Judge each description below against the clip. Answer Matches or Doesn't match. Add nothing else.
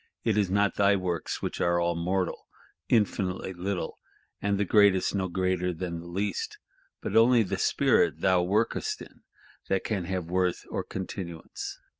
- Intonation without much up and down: Matches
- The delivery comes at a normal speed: Matches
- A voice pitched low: Matches